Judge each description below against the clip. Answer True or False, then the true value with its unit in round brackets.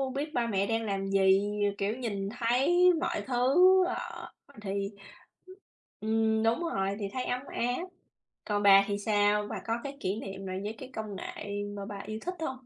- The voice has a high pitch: True (210 Hz)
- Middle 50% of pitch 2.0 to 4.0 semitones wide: True (3.7 semitones)